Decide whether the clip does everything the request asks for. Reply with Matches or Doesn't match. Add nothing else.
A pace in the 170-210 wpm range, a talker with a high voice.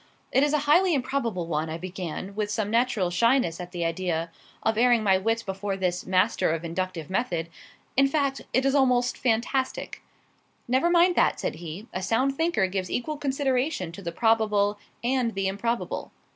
Matches